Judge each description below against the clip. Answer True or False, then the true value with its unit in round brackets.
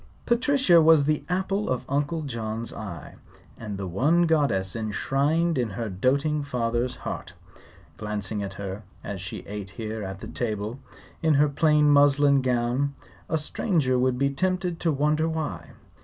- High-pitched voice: False (135 Hz)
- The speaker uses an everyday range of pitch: False (6.2 semitones)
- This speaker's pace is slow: False (150 wpm)